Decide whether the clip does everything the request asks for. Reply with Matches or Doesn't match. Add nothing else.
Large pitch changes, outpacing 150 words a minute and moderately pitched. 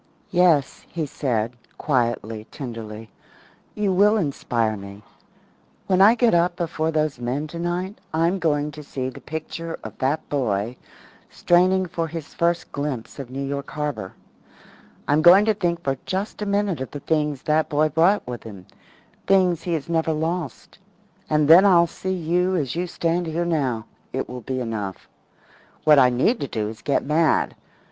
Doesn't match